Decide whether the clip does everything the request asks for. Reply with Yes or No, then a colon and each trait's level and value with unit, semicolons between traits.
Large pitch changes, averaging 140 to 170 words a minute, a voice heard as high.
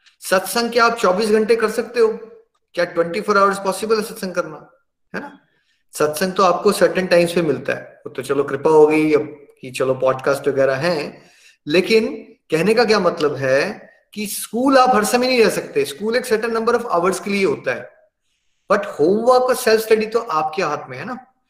No: wide, 6.4 semitones; average, 185 wpm; high, 205 Hz